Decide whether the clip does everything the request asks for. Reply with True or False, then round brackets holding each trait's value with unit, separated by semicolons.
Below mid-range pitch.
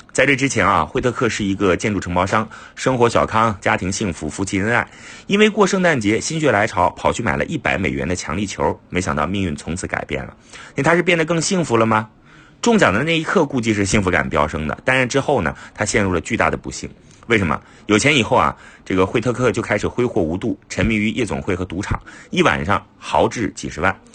True (110 Hz)